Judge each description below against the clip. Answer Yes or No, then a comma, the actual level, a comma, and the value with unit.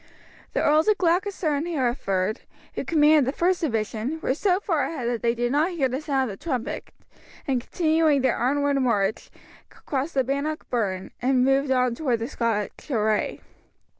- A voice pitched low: No, very high, 270 Hz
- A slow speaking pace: No, average, 175 wpm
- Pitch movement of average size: Yes, average, 4.7 semitones